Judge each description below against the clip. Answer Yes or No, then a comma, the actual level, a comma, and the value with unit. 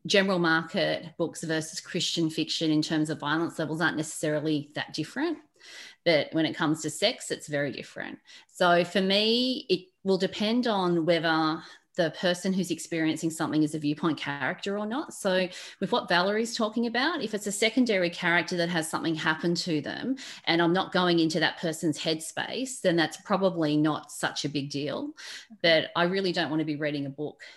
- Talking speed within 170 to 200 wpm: Yes, average, 185 wpm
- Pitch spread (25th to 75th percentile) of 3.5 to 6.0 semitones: Yes, average, 4.1 semitones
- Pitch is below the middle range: No, medium, 170 Hz